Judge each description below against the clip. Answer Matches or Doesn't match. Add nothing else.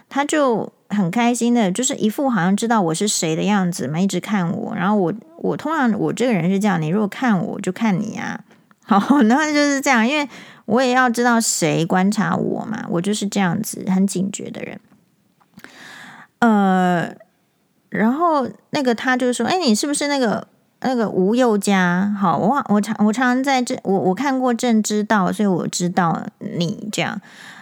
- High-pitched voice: Matches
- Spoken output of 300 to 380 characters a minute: Doesn't match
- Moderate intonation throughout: Matches